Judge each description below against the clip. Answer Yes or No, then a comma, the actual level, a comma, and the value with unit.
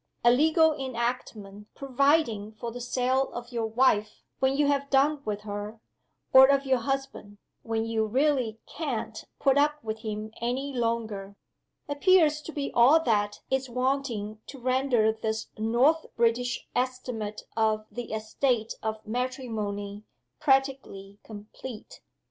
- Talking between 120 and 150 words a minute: Yes, slow, 135 wpm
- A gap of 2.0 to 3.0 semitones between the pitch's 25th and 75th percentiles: No, average, 3.7 semitones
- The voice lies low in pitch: No, high, 240 Hz